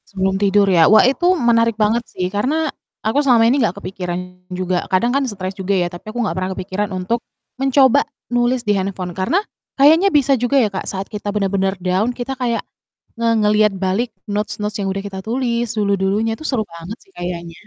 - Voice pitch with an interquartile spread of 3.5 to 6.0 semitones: Yes, average, 4.0 semitones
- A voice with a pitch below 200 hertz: No, high, 210 Hz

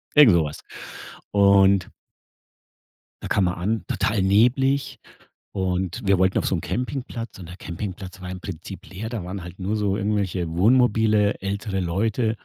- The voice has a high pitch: No, low, 100 Hz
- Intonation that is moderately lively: Yes, average, 3.1 semitones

